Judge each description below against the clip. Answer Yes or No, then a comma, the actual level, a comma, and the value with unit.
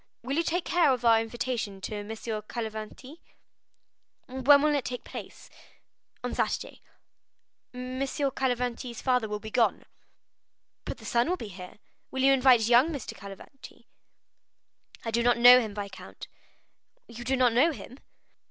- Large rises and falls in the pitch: No, average, 3.1 semitones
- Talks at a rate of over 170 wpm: No, average, 150 wpm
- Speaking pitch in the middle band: No, high, 245 Hz